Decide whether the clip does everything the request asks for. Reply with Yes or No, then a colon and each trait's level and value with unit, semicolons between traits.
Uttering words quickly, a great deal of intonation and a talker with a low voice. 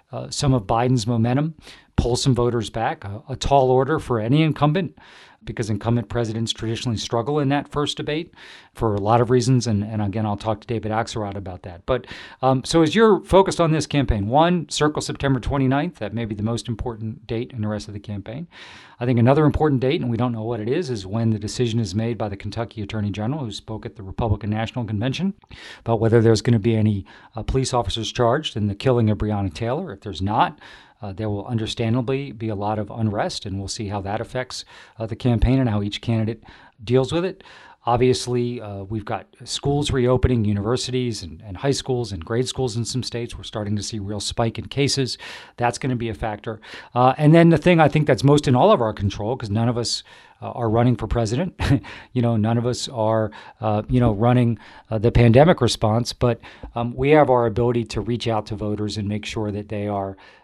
No: fast, 225 wpm; average, 3.2 semitones; low, 115 Hz